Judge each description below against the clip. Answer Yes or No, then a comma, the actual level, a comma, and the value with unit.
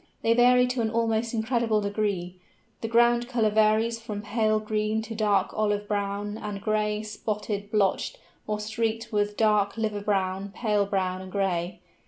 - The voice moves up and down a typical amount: No, narrow, 1.7 semitones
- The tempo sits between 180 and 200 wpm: No, average, 160 wpm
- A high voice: Yes, high, 215 Hz